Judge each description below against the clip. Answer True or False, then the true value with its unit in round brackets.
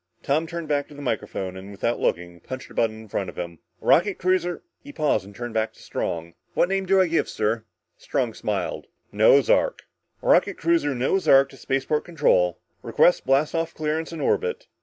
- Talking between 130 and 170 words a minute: False (200 wpm)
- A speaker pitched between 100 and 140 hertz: True (135 Hz)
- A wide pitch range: True (7.3 semitones)